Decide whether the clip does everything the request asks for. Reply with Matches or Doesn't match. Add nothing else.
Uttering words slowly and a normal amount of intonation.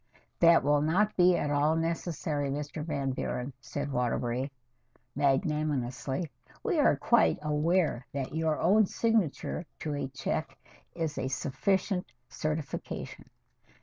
Matches